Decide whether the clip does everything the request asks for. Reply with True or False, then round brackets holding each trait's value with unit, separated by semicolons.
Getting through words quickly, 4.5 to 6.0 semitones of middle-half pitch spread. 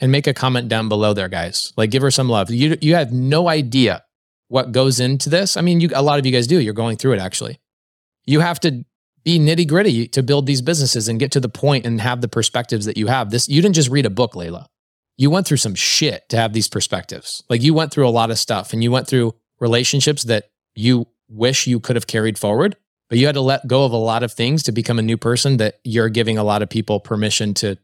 False (260 wpm; 3.9 semitones)